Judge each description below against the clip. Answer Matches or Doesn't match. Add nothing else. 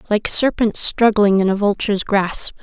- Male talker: Doesn't match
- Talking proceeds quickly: Doesn't match